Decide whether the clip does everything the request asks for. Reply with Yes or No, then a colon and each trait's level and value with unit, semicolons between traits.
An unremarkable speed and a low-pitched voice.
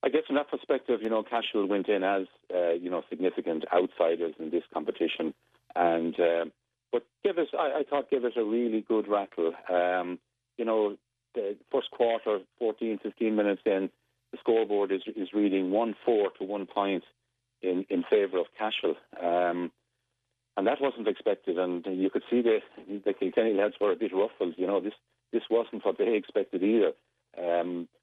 Yes: average, 180 wpm; low, 105 Hz